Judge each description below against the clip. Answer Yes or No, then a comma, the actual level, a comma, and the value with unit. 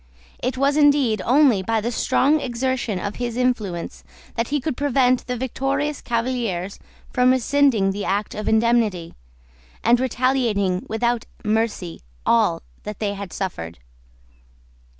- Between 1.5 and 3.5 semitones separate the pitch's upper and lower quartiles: No, average, 4.0 semitones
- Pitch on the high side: Yes, high, 235 Hz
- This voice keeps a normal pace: No, slow, 130 wpm